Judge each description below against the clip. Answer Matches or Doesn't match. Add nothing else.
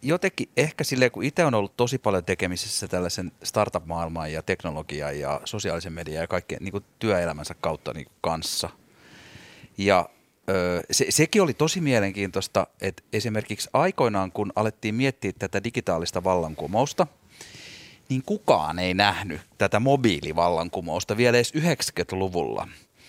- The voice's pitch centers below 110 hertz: Matches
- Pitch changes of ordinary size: Doesn't match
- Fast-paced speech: Doesn't match